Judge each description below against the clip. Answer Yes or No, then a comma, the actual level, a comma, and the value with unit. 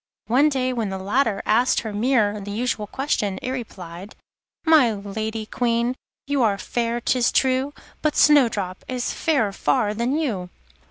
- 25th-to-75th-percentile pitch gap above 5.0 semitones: No, average, 4.0 semitones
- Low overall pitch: No, high, 230 Hz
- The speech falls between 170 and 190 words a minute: No, average, 155 wpm